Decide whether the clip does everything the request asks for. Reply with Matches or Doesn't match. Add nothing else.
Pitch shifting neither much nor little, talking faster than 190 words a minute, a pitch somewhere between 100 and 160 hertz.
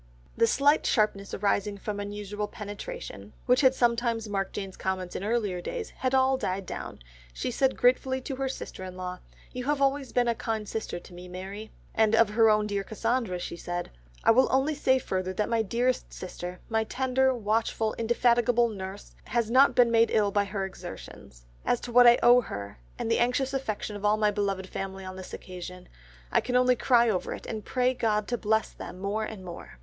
Doesn't match